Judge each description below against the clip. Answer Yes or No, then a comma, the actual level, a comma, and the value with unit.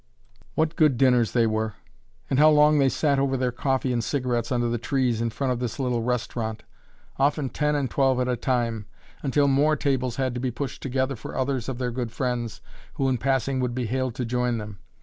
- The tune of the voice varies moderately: No, narrow, 2.3 semitones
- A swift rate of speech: Yes, fast, 215 wpm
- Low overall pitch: Yes, low, 125 Hz